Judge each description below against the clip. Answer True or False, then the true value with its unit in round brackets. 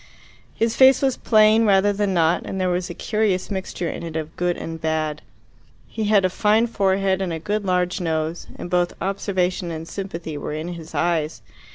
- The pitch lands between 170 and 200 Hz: True (185 Hz)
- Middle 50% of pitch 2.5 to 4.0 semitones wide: True (3.7 semitones)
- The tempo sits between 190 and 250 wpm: True (195 wpm)